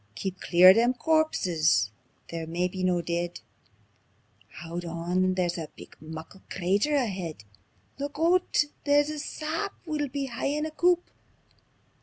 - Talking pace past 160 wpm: No, slow, 135 wpm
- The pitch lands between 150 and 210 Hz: Yes, high, 190 Hz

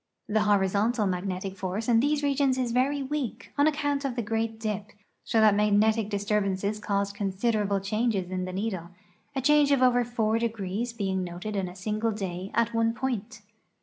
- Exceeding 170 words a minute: Yes, average, 180 wpm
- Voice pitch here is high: Yes, high, 215 Hz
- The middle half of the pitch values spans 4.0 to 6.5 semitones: No, average, 3.4 semitones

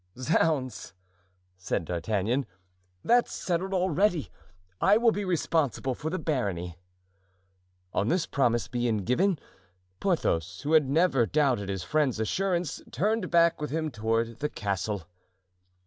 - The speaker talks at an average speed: No, slow, 125 wpm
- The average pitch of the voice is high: No, medium, 140 Hz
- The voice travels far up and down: Yes, wide, 7.6 semitones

